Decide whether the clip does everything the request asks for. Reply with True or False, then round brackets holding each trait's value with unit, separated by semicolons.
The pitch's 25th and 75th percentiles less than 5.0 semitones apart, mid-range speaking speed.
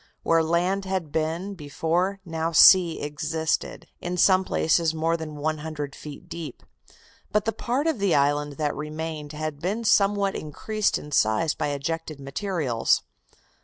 True (3.9 semitones; 150 wpm)